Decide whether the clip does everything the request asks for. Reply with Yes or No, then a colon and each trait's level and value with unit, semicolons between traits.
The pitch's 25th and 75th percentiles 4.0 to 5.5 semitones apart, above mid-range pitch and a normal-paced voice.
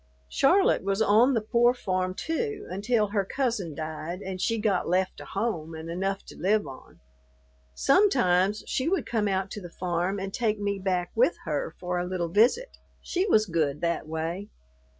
Yes: average, 4.4 semitones; high, 195 Hz; average, 180 wpm